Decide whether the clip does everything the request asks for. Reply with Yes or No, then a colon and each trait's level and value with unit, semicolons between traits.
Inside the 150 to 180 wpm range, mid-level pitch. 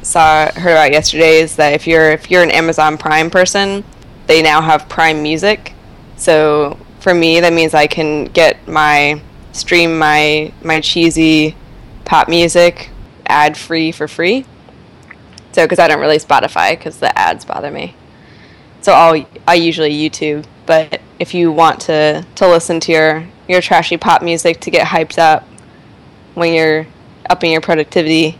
Yes: average, 160 wpm; medium, 160 Hz